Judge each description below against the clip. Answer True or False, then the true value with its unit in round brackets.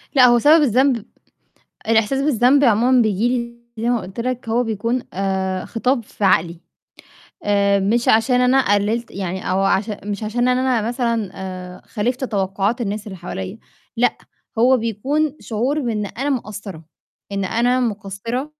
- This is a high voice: True (225 Hz)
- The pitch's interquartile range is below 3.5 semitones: False (3.8 semitones)